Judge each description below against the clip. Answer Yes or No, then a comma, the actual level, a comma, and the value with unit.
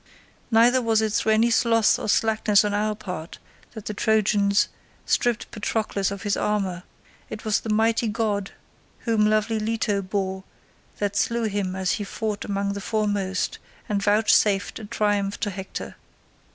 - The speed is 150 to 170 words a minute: Yes, average, 155 wpm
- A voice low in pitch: No, high, 210 Hz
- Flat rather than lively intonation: Yes, narrow, 1.7 semitones